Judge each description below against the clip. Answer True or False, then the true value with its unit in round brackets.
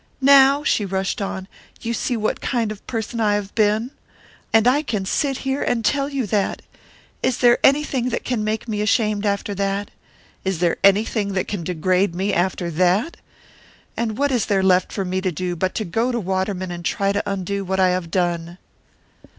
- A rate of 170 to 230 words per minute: True (195 wpm)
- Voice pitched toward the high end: True (205 Hz)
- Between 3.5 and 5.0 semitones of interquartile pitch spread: True (3.8 semitones)